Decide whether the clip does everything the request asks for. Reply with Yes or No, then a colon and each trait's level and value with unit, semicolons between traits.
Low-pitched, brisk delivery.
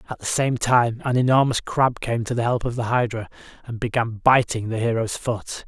Yes: low, 120 Hz; fast, 210 wpm